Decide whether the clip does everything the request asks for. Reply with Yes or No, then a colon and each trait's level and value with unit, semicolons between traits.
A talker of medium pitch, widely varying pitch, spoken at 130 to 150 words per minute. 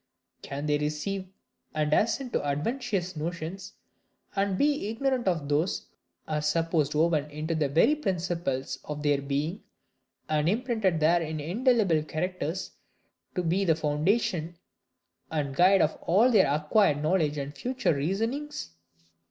No: medium, 165 Hz; average, 4.7 semitones; slow, 135 wpm